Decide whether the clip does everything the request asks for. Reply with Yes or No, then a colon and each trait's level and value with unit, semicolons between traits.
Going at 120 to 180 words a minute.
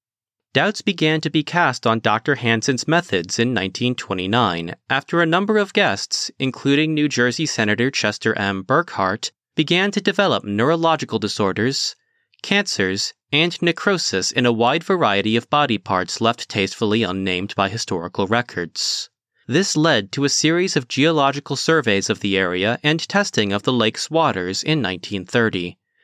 Yes: average, 145 wpm